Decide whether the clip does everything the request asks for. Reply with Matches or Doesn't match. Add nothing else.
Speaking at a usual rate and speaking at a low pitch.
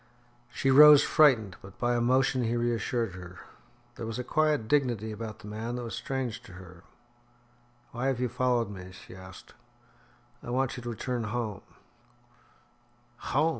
Matches